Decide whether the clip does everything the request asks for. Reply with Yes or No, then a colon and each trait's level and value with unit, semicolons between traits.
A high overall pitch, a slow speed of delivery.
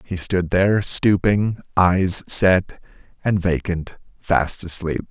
No: very low, 90 Hz; slow, 120 wpm